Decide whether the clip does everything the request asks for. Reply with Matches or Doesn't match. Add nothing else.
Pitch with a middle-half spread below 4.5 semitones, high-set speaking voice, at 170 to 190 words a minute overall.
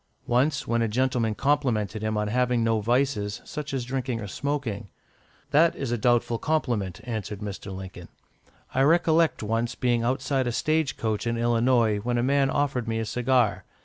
Doesn't match